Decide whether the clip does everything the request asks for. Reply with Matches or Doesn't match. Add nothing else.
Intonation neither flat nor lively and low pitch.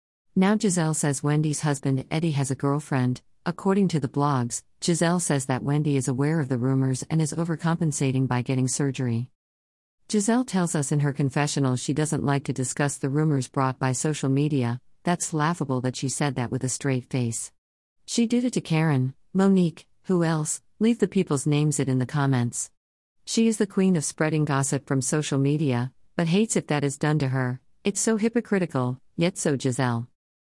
Doesn't match